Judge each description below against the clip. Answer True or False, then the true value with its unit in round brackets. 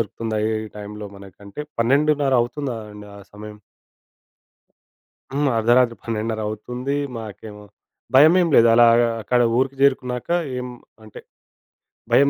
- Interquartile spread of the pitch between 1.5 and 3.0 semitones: False (4.0 semitones)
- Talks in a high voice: False (120 Hz)